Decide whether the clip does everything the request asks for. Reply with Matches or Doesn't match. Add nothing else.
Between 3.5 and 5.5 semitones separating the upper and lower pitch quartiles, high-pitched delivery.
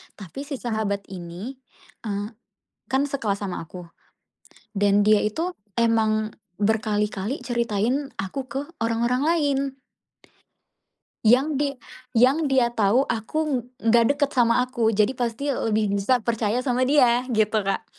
Matches